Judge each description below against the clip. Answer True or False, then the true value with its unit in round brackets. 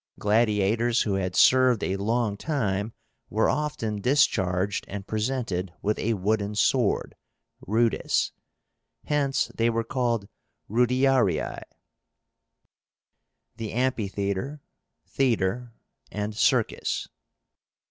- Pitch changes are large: False (3.7 semitones)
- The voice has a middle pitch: False (110 Hz)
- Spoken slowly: True (90 wpm)